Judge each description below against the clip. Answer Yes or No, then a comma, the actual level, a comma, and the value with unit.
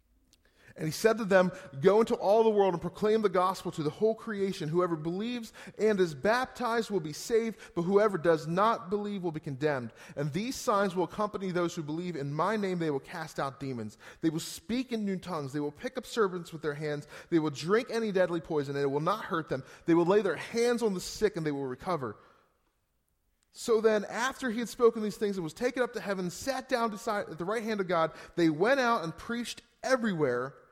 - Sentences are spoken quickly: Yes, fast, 230 wpm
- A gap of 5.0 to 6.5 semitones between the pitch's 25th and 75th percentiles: Yes, average, 5.3 semitones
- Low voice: No, medium, 185 Hz